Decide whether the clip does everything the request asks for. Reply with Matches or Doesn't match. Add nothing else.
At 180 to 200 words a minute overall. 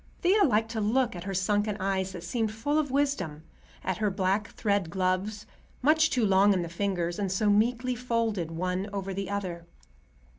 Matches